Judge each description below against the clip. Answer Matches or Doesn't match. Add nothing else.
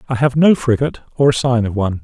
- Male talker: Matches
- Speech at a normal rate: Doesn't match